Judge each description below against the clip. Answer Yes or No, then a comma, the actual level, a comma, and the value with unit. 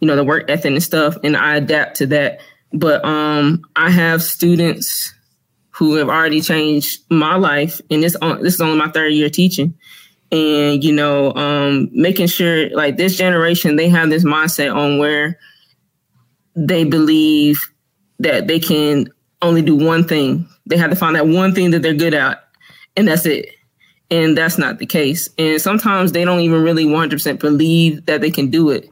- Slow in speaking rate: No, average, 185 wpm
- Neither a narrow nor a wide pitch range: No, narrow, 2.0 semitones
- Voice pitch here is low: No, medium, 160 Hz